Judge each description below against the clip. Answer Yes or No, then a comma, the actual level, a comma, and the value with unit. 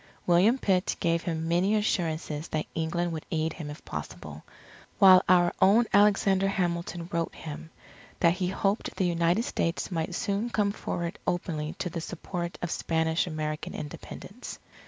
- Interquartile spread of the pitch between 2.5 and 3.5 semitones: Yes, average, 2.8 semitones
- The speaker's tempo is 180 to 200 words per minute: No, average, 155 wpm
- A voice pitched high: No, medium, 175 Hz